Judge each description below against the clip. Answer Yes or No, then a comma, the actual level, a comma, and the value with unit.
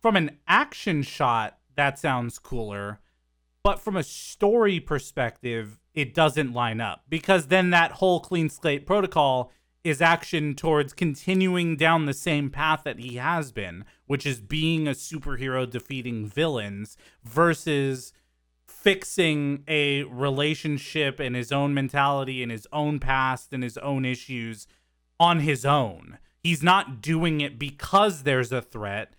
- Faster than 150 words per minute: No, average, 140 wpm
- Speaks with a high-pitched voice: No, medium, 140 Hz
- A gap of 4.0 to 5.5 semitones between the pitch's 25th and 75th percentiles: Yes, average, 4.6 semitones